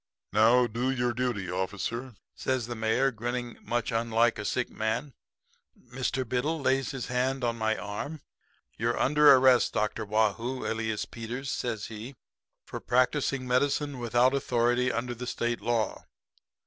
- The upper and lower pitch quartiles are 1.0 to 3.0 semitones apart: Yes, narrow, 2.4 semitones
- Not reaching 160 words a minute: Yes, average, 150 wpm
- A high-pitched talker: No, low, 120 Hz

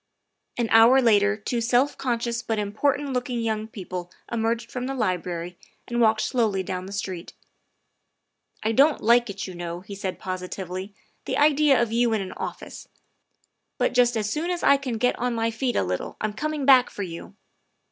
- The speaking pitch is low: No, high, 225 Hz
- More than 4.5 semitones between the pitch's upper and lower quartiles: No, average, 4.1 semitones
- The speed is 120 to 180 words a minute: No, average, 195 wpm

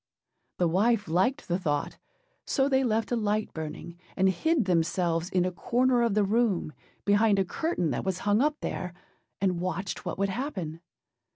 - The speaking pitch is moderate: No, high, 195 Hz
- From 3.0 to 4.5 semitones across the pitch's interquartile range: No, average, 5.0 semitones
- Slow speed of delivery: No, average, 180 wpm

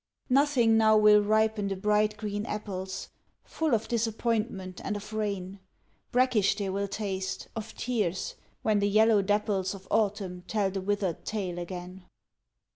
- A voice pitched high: Yes, high, 205 Hz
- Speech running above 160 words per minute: No, average, 145 wpm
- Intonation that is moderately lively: No, narrow, 2.2 semitones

